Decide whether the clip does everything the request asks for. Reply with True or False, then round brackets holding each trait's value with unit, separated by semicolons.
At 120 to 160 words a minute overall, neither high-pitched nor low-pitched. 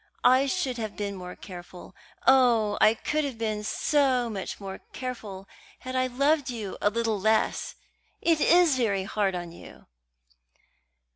False (150 wpm; 225 Hz)